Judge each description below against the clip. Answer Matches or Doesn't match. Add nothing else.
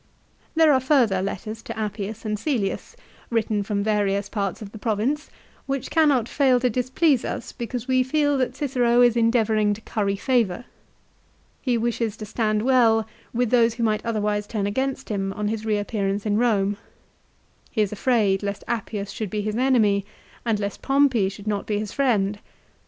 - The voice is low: Doesn't match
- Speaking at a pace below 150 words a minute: Doesn't match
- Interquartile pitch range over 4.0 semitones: Doesn't match